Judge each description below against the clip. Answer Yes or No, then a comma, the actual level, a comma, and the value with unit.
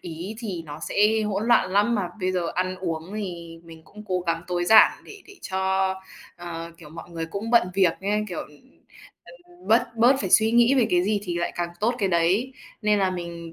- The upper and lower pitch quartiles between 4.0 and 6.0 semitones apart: No, average, 3.6 semitones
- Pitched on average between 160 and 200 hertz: Yes, medium, 185 Hz